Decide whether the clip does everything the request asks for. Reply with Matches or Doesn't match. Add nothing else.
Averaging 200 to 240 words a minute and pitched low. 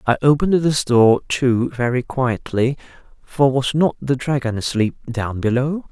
Doesn't match